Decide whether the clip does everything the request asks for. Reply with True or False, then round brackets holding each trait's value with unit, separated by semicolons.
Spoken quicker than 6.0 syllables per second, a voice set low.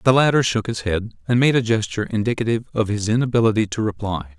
True (6.6 syllables/s; 110 Hz)